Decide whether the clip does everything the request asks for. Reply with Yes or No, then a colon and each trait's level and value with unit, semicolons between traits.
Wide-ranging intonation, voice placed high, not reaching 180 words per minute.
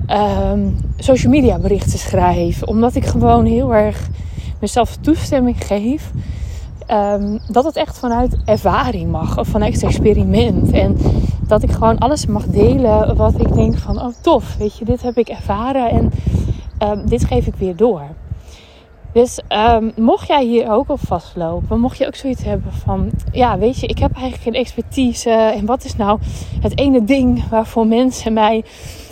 Yes: wide, 6.2 semitones; high, 225 Hz; average, 170 wpm